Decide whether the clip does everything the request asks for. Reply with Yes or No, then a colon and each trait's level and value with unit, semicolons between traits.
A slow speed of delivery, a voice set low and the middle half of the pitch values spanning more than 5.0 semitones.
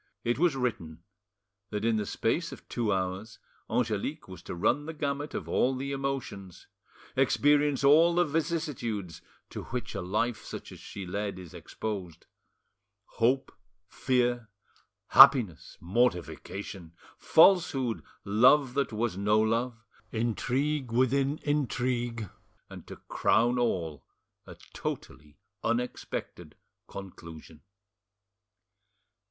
Yes: slow, 115 wpm; low, 120 Hz; wide, 5.5 semitones